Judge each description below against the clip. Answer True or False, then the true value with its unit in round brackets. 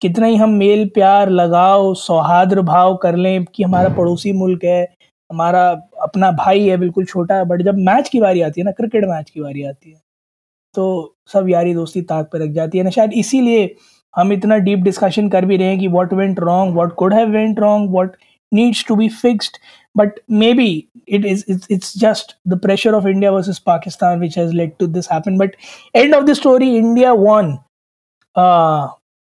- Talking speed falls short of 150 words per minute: False (190 wpm)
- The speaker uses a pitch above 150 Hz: True (190 Hz)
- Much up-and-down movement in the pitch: False (3.0 semitones)